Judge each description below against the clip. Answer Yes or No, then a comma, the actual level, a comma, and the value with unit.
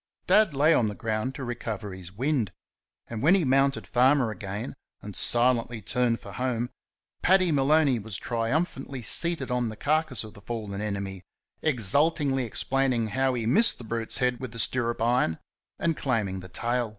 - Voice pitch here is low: Yes, low, 120 Hz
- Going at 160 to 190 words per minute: Yes, average, 170 wpm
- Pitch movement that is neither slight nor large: Yes, average, 3.8 semitones